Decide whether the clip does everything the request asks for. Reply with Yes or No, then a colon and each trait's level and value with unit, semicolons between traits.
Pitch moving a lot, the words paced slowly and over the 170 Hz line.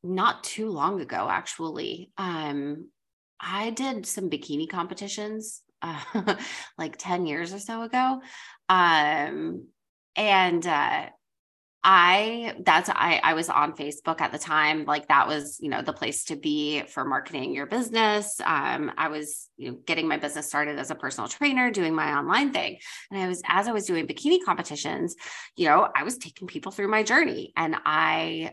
No: wide, 6.0 semitones; average, 170 wpm; medium, 185 Hz